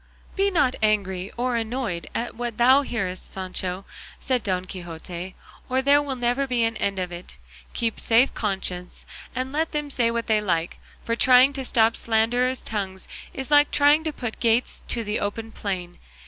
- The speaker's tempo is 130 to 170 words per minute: No, average, 180 wpm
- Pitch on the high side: Yes, high, 230 Hz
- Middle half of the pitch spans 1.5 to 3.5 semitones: No, average, 5.1 semitones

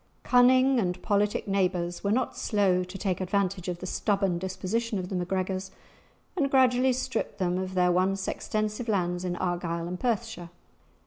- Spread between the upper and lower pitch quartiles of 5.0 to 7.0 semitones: No, average, 3.3 semitones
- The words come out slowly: No, average, 165 wpm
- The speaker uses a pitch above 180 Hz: Yes, high, 190 Hz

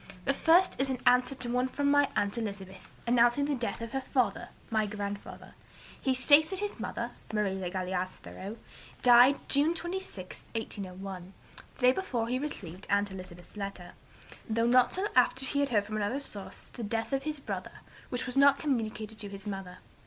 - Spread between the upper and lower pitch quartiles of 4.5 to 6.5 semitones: Yes, average, 5.1 semitones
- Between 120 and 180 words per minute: No, average, 190 wpm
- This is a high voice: Yes, high, 235 Hz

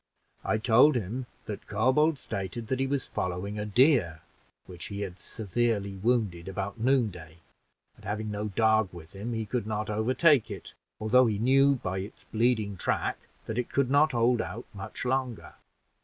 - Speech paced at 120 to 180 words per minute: Yes, average, 170 wpm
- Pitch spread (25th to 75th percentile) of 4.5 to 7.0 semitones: No, average, 4.0 semitones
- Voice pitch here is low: Yes, low, 110 Hz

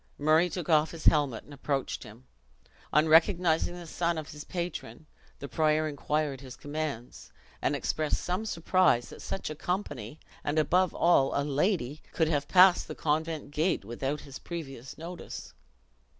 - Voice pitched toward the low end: No, medium, 155 Hz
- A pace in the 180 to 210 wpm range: No, average, 160 wpm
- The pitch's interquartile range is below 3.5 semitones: Yes, average, 3.1 semitones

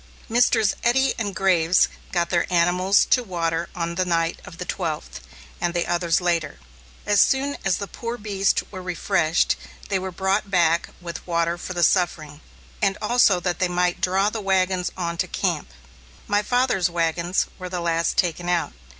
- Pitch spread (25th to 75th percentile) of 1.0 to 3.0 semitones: Yes, narrow, 2.5 semitones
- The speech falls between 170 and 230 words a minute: Yes, average, 175 wpm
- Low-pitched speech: No, medium, 180 Hz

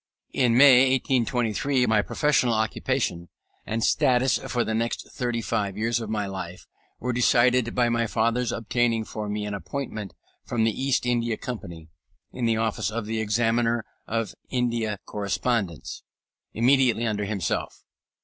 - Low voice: Yes, low, 115 Hz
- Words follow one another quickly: No, average, 145 wpm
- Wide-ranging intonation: No, narrow, 2.4 semitones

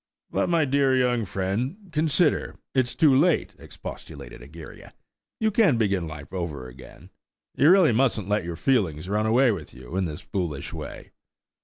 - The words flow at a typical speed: Yes, average, 155 wpm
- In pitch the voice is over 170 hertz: No, low, 110 Hz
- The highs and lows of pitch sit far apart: Yes, wide, 8.2 semitones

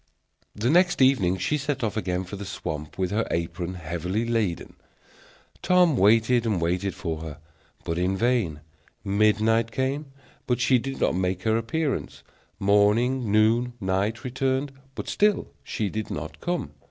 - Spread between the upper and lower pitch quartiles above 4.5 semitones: Yes, average, 5.3 semitones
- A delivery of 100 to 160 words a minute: Yes, average, 155 wpm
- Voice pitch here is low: Yes, low, 110 Hz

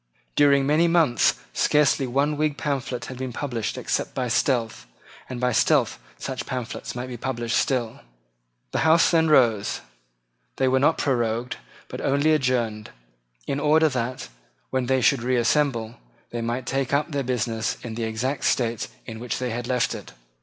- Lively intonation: No, average, 3.1 semitones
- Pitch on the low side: Yes, low, 130 Hz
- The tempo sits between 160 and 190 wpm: Yes, average, 165 wpm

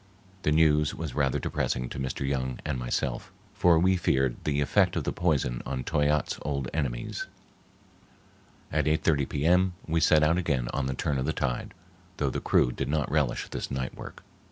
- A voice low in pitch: Yes, very low, 70 Hz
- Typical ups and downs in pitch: Yes, average, 3.1 semitones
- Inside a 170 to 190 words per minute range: Yes, average, 180 wpm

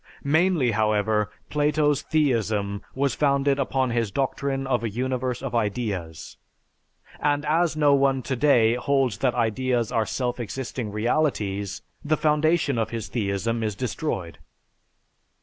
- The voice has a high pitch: No, low, 125 Hz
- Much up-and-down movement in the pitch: No, average, 4.3 semitones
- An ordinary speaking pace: No, slow, 130 wpm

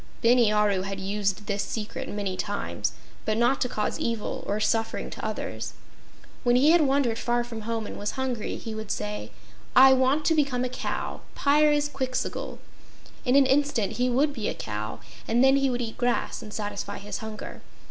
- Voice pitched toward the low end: No, high, 235 Hz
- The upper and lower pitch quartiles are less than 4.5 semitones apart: Yes, average, 4.1 semitones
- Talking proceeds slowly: No, average, 185 wpm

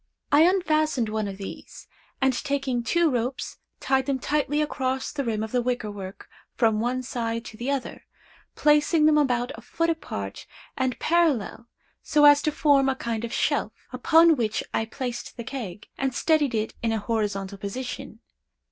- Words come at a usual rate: Yes, average, 175 wpm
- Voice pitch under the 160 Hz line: No, very high, 255 Hz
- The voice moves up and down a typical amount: Yes, average, 4.6 semitones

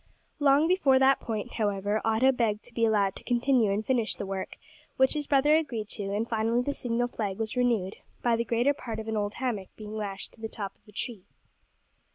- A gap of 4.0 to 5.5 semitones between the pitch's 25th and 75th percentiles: No, average, 3.4 semitones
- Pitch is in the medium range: No, high, 225 Hz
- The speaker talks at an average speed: No, fast, 215 wpm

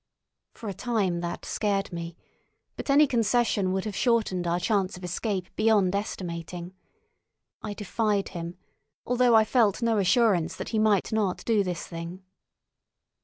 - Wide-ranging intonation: No, average, 3.8 semitones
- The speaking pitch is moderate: No, high, 200 Hz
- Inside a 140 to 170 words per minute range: Yes, average, 150 wpm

